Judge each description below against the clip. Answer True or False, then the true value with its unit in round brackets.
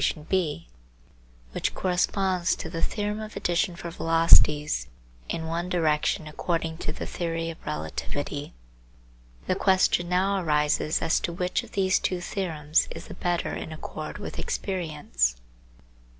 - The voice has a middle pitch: True (165 Hz)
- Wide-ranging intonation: False (3.0 semitones)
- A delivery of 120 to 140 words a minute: True (135 wpm)